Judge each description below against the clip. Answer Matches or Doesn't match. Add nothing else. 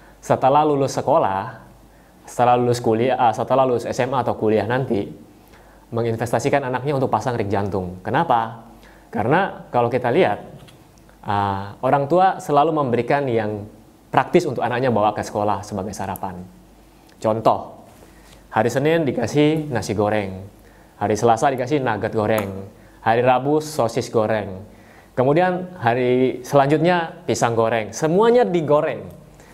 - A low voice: Matches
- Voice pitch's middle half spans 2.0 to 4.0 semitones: Doesn't match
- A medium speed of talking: Matches